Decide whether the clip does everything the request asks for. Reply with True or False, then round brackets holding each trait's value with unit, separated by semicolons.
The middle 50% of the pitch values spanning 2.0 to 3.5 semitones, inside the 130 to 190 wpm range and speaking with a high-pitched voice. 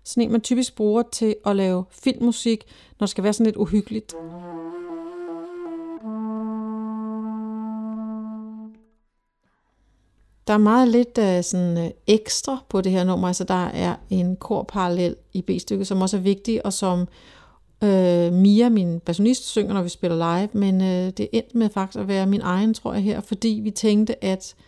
True (2.9 semitones; 165 wpm; 215 Hz)